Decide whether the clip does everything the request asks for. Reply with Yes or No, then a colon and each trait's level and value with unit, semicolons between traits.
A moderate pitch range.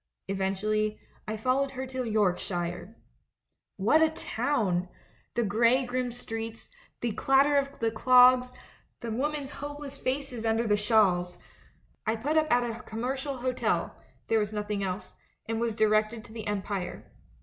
Yes: average, 3.5 semitones